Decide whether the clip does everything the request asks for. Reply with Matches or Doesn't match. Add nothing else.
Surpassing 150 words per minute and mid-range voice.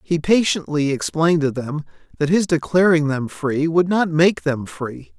Matches